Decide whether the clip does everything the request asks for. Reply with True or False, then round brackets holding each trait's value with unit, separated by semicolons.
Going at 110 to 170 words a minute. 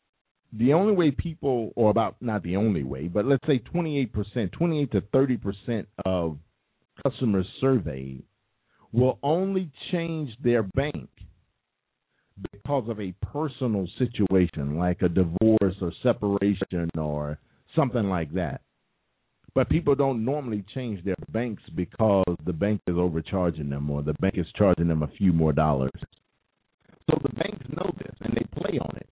True (150 wpm)